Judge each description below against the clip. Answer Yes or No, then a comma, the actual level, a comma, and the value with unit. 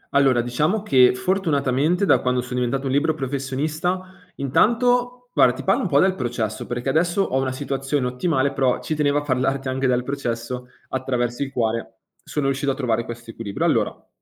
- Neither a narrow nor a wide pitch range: Yes, average, 3.3 semitones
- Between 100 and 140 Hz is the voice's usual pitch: Yes, low, 135 Hz